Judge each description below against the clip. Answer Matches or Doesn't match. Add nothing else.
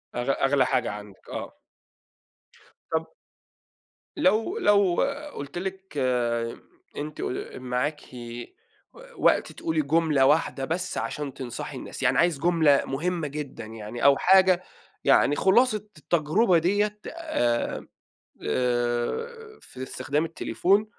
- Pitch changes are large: Matches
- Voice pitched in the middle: Matches